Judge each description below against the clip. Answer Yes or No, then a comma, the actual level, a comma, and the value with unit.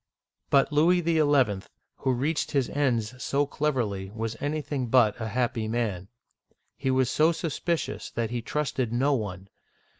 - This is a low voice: Yes, low, 130 Hz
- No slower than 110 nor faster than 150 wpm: Yes, average, 145 wpm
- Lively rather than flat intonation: No, average, 4.5 semitones